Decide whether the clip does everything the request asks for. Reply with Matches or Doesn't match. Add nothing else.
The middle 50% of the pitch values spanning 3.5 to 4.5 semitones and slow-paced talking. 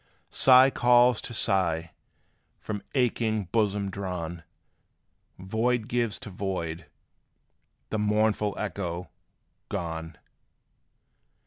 Matches